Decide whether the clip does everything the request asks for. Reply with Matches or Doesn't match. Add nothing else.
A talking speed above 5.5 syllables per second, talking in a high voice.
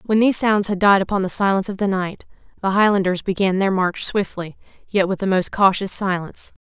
Matches